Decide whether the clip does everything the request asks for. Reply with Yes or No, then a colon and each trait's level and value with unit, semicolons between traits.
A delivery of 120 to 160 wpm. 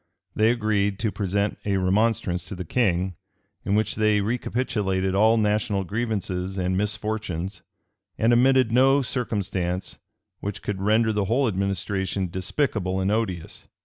Yes: slow, 135 wpm